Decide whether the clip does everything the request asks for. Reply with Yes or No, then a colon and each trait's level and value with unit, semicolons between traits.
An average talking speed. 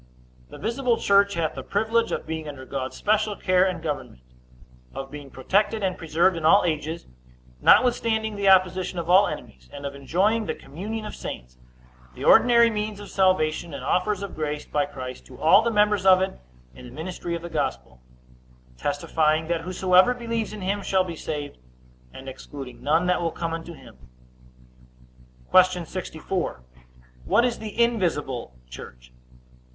Yes: average, 165 wpm